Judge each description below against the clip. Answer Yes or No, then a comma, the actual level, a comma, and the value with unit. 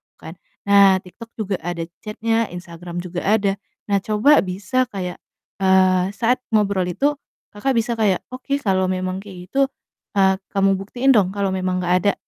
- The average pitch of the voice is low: No, high, 195 Hz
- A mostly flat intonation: No, average, 3.2 semitones